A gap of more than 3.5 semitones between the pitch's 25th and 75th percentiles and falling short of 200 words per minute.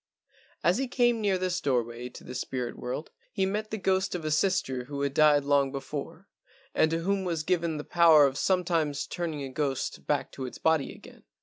No: average, 5.0 semitones; fast, 205 wpm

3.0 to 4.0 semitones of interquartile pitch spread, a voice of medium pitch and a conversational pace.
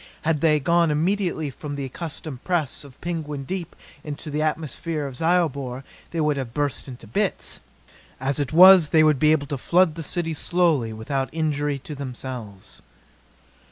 Yes: average, 3.3 semitones; medium, 150 Hz; average, 165 wpm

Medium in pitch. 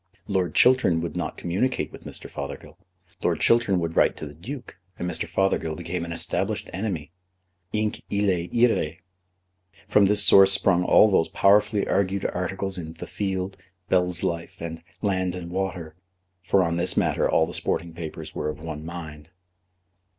No: very low, 90 Hz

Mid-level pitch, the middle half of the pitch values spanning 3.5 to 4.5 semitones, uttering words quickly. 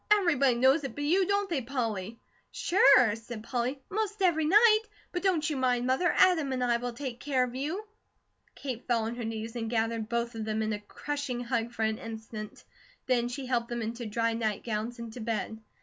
No: high, 245 Hz; average, 4.0 semitones; fast, 210 wpm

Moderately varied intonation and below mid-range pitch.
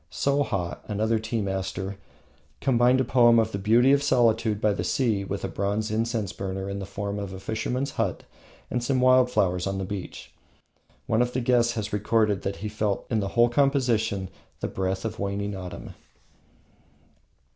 Yes: average, 3.4 semitones; low, 110 Hz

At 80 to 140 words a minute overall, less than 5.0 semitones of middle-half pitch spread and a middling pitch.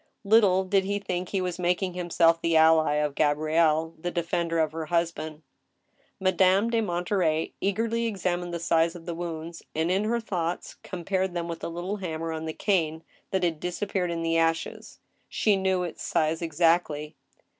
No: average, 175 wpm; narrow, 2.5 semitones; medium, 170 Hz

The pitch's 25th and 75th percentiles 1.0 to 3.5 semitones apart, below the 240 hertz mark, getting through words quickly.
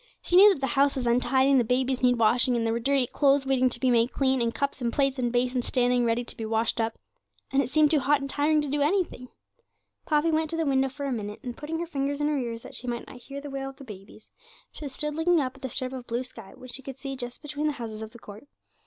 No: average, 2.9 semitones; very high, 265 Hz; fast, 285 wpm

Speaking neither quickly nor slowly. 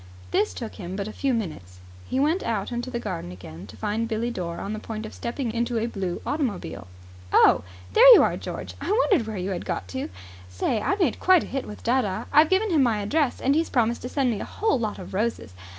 No: fast, 240 wpm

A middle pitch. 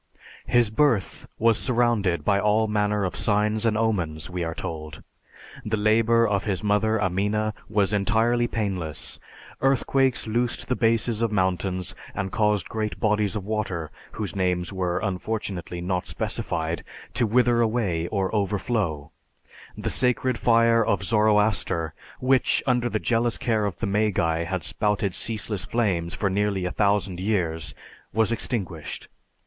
No: low, 105 Hz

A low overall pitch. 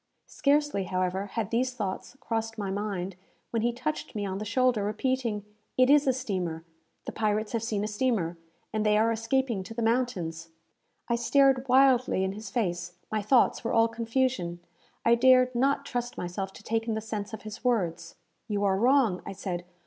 No: high, 220 Hz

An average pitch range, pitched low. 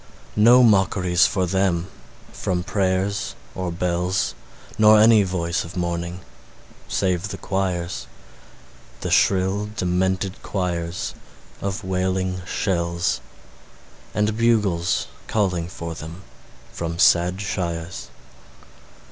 No: narrow, 2.2 semitones; very low, 95 Hz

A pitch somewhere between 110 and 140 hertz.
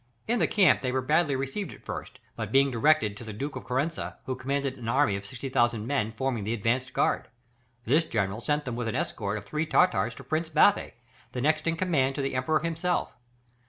Yes: low, 135 Hz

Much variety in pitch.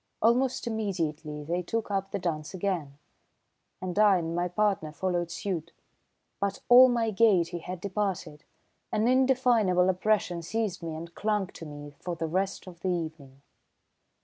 No: average, 4.1 semitones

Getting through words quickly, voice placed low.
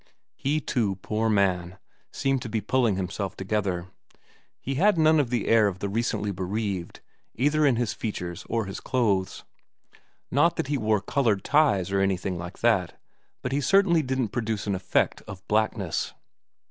No: average, 165 wpm; low, 110 Hz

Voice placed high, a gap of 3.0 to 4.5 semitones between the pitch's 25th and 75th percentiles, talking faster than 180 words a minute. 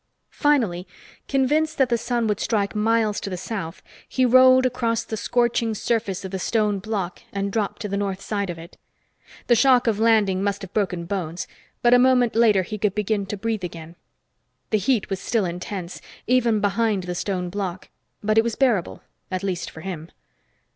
Yes: high, 210 Hz; average, 3.5 semitones; average, 190 wpm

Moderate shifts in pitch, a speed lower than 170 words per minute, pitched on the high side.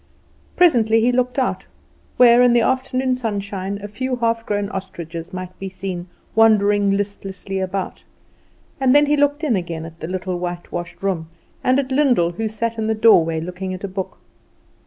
No: average, 4.9 semitones; average, 175 wpm; high, 205 Hz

